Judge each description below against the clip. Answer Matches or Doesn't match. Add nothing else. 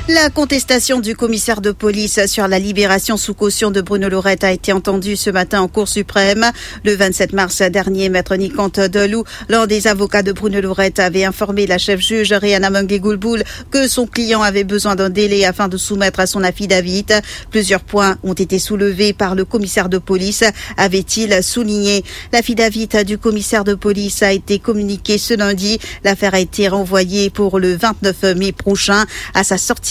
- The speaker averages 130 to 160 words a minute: Doesn't match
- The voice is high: Matches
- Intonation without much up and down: Matches